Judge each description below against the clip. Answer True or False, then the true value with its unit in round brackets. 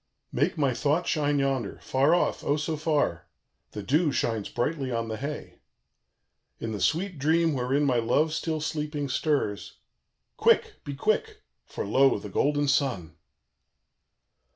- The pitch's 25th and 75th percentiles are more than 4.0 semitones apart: False (3.7 semitones)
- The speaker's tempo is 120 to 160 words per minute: True (145 wpm)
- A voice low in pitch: False (145 Hz)